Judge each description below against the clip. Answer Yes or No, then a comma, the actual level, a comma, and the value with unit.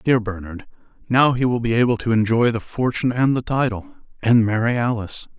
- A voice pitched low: Yes, low, 115 Hz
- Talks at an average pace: Yes, average, 190 wpm